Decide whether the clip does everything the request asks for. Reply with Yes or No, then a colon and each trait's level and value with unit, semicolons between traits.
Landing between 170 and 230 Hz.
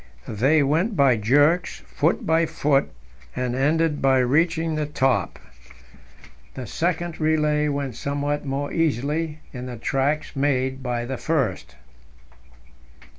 No: medium, 145 Hz